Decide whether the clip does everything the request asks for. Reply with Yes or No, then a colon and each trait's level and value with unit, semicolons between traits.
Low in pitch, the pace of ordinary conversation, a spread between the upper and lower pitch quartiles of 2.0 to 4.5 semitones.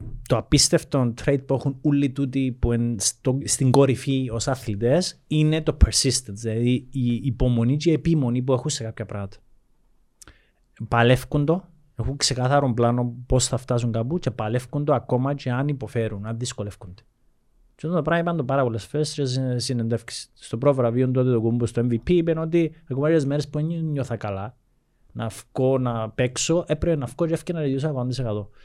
Yes: low, 130 Hz; average, 160 wpm; average, 3.7 semitones